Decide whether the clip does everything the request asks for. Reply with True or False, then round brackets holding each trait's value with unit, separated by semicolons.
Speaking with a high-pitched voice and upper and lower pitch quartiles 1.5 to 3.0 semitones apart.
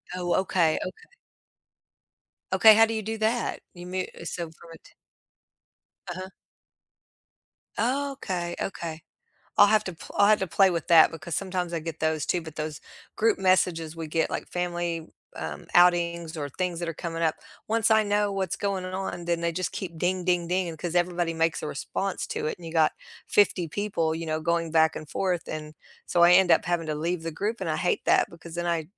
False (175 Hz; 2.5 semitones)